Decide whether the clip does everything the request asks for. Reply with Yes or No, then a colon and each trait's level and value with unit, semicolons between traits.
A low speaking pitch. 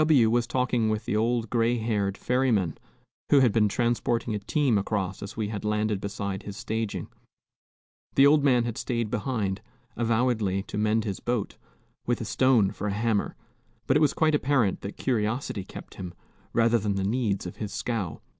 Yes: low, 110 Hz